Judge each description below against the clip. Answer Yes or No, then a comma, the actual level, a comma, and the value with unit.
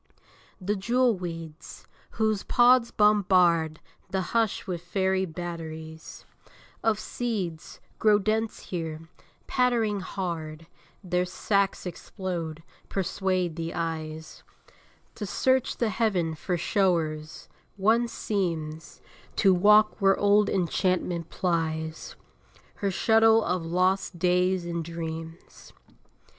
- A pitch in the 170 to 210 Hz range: Yes, medium, 185 Hz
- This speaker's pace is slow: Yes, slow, 100 wpm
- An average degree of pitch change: Yes, average, 4.0 semitones